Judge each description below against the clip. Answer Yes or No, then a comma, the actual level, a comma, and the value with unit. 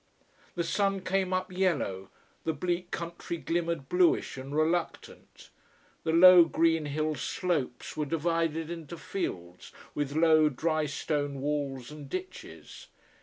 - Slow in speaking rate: Yes, slow, 125 wpm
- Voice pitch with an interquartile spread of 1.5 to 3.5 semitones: Yes, average, 3.0 semitones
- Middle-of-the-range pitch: Yes, medium, 160 Hz